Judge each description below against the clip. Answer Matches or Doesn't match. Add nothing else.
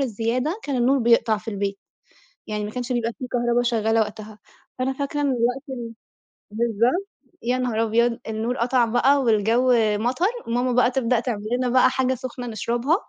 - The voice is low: Doesn't match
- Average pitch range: Doesn't match